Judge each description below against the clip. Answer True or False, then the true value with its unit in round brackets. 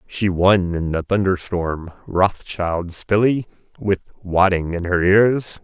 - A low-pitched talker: True (95 Hz)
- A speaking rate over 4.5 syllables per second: False (3.5 syllables/s)